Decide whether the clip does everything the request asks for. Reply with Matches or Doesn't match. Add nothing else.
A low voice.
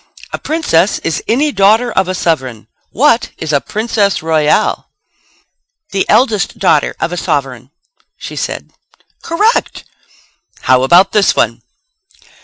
Doesn't match